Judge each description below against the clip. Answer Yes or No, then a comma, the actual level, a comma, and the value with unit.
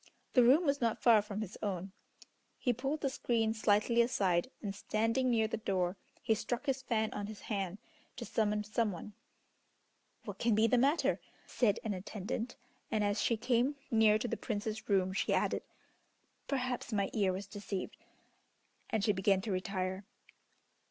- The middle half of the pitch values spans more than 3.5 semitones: No, average, 2.9 semitones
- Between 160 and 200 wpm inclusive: Yes, average, 170 wpm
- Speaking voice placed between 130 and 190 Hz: No, high, 215 Hz